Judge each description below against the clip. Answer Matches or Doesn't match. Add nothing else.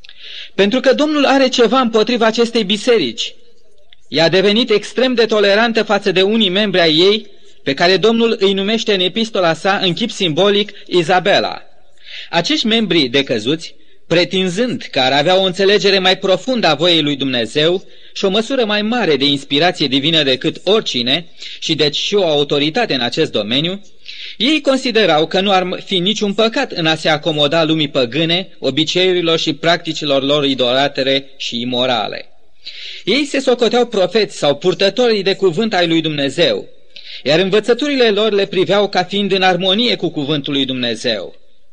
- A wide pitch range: Matches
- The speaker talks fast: Doesn't match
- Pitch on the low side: Doesn't match